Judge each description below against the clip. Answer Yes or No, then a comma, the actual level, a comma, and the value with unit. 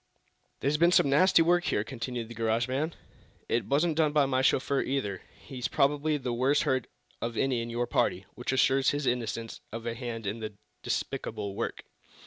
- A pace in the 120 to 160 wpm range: No, average, 185 wpm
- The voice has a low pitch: Yes, low, 130 Hz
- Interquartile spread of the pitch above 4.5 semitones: No, average, 3.6 semitones